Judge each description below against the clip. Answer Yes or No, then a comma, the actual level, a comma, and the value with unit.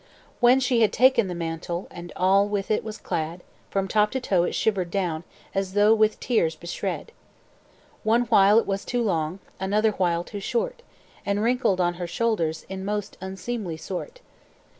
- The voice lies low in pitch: No, high, 200 Hz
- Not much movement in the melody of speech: No, average, 3.9 semitones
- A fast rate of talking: No, average, 175 wpm